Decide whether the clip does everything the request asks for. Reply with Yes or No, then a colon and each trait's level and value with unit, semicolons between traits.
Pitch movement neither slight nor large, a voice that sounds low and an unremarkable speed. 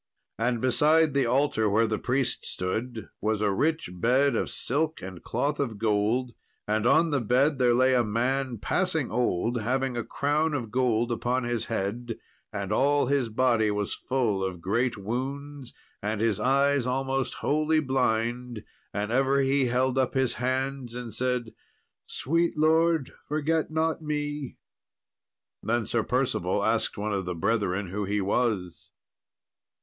Yes: average, 3.9 semitones; low, 125 Hz; average, 155 wpm